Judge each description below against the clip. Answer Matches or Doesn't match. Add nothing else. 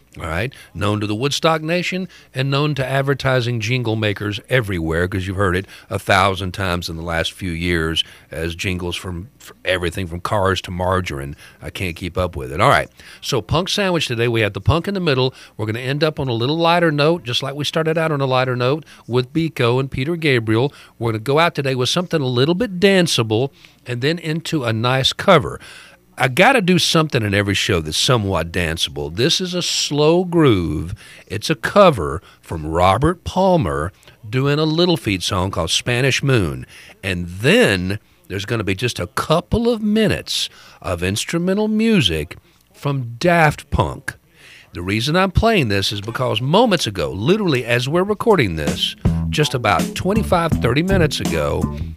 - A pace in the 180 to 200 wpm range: Matches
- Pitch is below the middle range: Matches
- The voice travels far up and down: Matches